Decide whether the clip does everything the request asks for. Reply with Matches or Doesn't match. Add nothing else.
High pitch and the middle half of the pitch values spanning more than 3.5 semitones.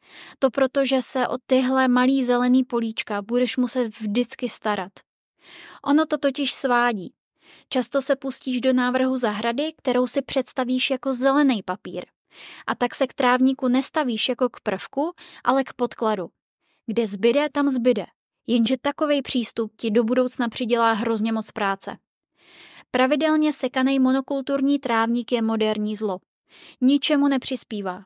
Doesn't match